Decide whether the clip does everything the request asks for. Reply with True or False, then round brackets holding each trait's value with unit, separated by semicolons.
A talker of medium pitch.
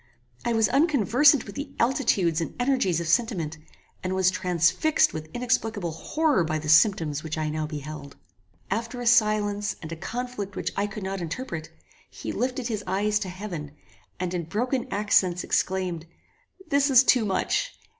False (200 Hz)